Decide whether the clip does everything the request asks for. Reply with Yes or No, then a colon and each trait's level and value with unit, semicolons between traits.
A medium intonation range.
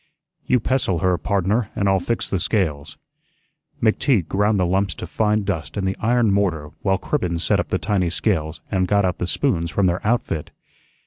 Yes: average, 3.1 semitones